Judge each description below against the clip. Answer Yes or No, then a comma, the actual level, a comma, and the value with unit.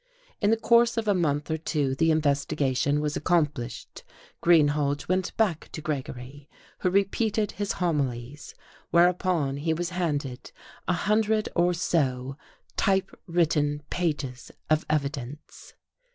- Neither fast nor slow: No, slow, 125 wpm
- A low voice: No, medium, 155 Hz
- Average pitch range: Yes, average, 4.1 semitones